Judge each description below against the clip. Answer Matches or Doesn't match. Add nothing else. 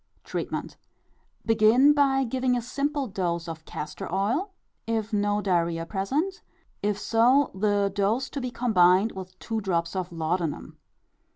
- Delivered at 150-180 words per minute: Doesn't match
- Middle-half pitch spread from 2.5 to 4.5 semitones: Doesn't match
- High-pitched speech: Matches